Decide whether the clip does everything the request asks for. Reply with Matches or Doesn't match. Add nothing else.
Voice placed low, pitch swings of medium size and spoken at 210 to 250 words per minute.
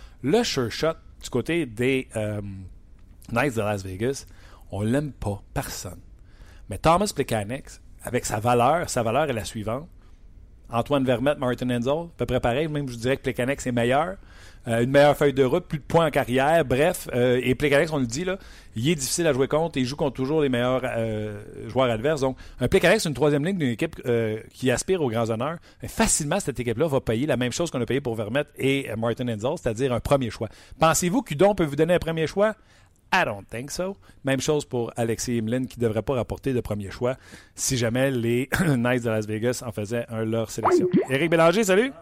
Matches